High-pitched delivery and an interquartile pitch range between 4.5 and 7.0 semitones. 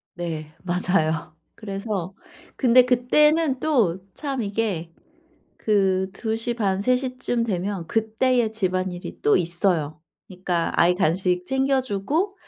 Yes: high, 200 Hz; wide, 5.6 semitones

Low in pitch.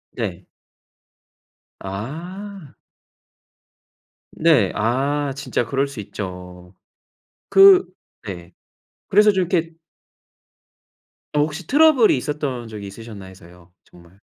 Yes: low, 130 Hz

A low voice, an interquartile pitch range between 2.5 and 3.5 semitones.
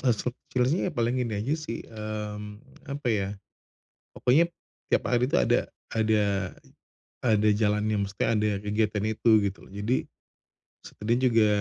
Yes: low, 110 Hz; average, 2.8 semitones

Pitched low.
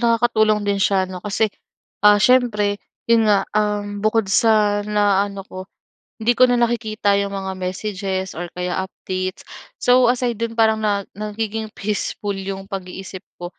No: high, 205 Hz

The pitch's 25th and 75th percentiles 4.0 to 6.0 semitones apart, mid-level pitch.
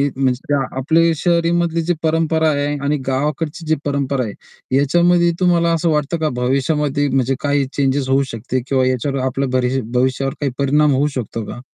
No: average, 3.2 semitones; medium, 145 Hz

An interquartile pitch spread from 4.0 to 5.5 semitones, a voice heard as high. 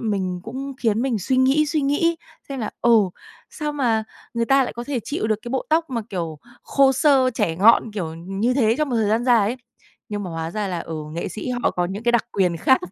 Yes: average, 5.2 semitones; high, 235 Hz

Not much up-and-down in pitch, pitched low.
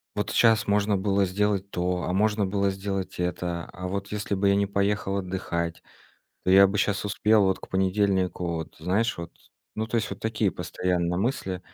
Yes: narrow, 2.1 semitones; low, 100 Hz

